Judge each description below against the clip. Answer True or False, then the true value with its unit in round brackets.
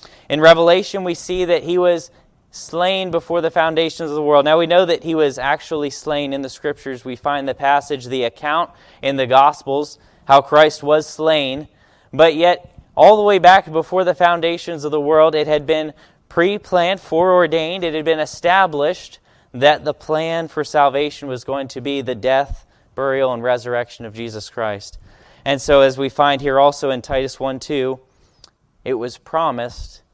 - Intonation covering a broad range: False (3.7 semitones)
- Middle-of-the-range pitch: True (150 Hz)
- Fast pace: False (175 wpm)